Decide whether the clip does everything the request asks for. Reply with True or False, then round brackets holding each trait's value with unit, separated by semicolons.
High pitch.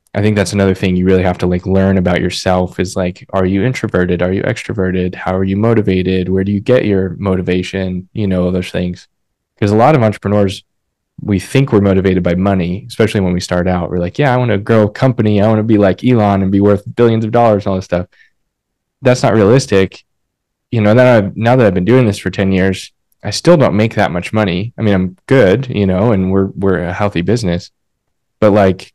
False (95 Hz)